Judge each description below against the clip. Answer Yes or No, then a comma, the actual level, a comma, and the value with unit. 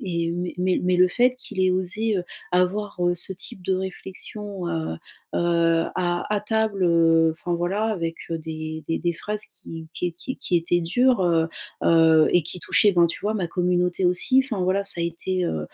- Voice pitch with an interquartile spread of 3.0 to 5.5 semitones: No, narrow, 2.4 semitones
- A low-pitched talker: No, medium, 180 Hz